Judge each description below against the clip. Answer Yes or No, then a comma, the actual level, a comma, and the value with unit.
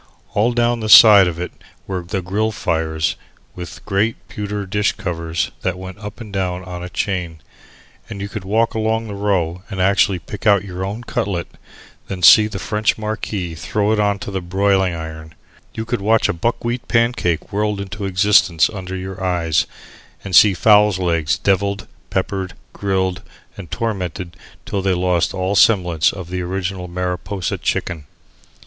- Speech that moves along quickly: No, average, 170 wpm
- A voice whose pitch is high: No, very low, 95 Hz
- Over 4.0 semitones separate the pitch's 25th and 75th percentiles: No, average, 2.7 semitones